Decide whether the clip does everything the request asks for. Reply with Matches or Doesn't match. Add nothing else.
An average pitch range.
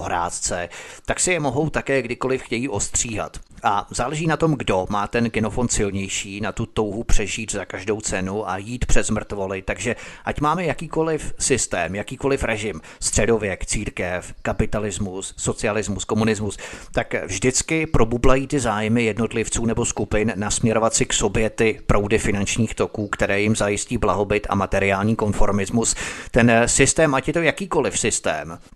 Matches